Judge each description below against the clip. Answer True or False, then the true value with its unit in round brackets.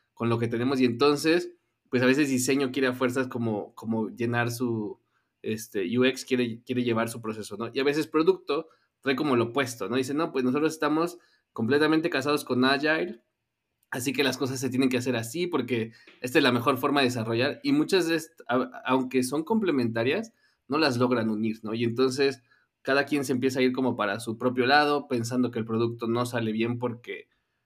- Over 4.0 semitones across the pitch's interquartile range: False (3.3 semitones)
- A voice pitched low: True (130 Hz)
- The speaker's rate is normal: False (200 wpm)